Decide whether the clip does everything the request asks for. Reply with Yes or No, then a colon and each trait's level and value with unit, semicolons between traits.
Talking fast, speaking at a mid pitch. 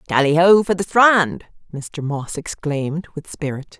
No: average, 160 wpm; medium, 160 Hz